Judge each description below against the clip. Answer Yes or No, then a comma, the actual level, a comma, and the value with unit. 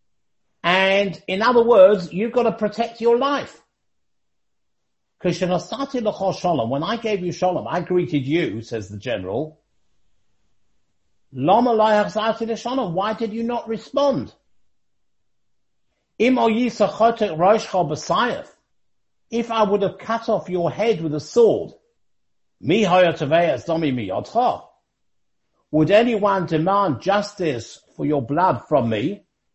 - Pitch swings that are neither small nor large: No, wide, 5.7 semitones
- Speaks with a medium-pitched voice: No, high, 200 Hz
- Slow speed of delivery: Yes, slow, 95 wpm